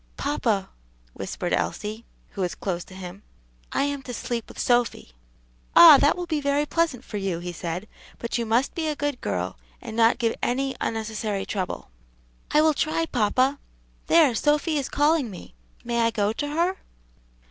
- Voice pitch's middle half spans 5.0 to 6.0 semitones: Yes, wide, 5.6 semitones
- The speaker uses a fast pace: No, average, 175 wpm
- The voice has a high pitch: Yes, high, 245 Hz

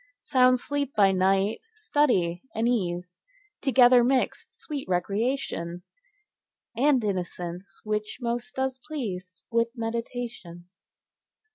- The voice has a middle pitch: No, high, 225 Hz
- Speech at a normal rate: No, slow, 100 wpm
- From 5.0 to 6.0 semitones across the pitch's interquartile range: Yes, wide, 5.6 semitones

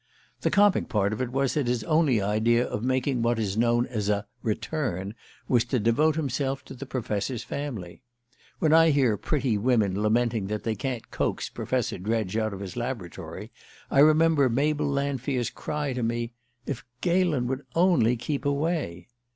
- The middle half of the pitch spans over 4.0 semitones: Yes, average, 4.5 semitones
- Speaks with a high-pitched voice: No, low, 125 Hz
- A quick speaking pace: No, average, 170 wpm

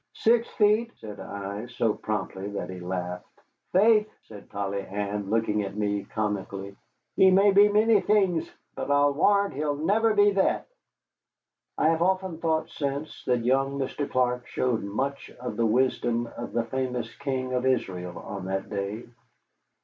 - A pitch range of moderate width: No, wide, 8.6 semitones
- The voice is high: No, low, 125 Hz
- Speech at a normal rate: Yes, average, 155 wpm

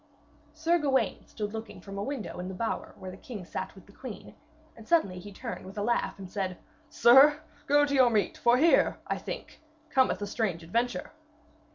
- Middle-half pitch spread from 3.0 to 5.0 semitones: No, wide, 5.4 semitones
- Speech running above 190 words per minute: Yes, average, 200 wpm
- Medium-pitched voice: No, high, 225 Hz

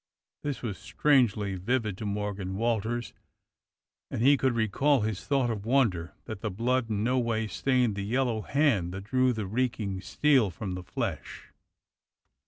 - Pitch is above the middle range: No, low, 110 Hz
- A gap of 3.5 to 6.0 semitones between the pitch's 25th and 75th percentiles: Yes, average, 4.2 semitones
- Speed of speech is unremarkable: Yes, average, 160 wpm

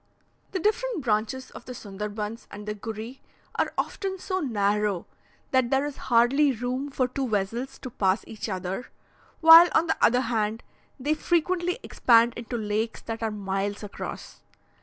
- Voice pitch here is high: Yes, high, 235 Hz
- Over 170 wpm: No, average, 160 wpm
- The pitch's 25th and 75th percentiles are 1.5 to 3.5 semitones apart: No, average, 4.6 semitones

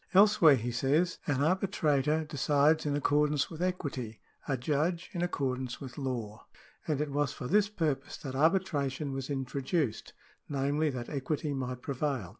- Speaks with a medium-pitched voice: Yes, medium, 145 Hz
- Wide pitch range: No, average, 3.0 semitones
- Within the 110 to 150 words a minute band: No, average, 165 wpm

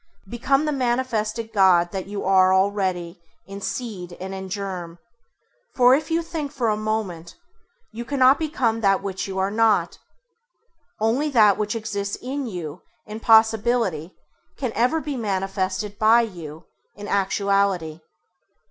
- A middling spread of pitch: Yes, average, 3.9 semitones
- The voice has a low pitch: No, high, 210 Hz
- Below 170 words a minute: Yes, average, 140 wpm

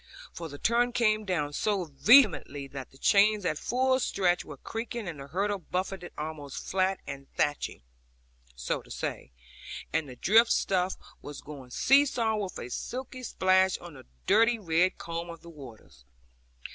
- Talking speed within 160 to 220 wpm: Yes, average, 165 wpm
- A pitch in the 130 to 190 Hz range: Yes, medium, 185 Hz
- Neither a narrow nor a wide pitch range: No, wide, 6.6 semitones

